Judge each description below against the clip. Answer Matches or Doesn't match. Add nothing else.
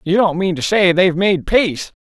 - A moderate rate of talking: Doesn't match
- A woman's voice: Doesn't match